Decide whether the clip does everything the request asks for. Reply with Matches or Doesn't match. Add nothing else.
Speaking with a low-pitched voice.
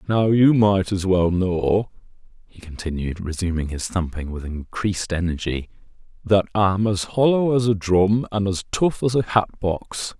Matches